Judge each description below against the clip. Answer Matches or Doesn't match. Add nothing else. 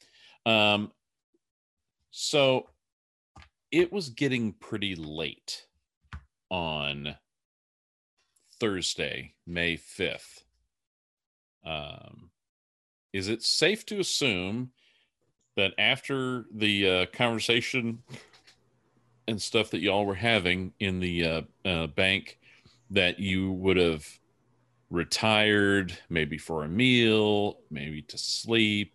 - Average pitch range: Doesn't match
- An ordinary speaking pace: Doesn't match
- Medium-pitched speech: Doesn't match